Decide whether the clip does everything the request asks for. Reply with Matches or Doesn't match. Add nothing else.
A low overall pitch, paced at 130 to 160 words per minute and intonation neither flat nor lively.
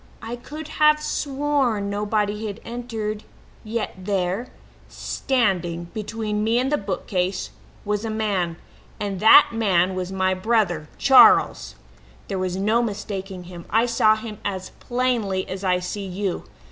Doesn't match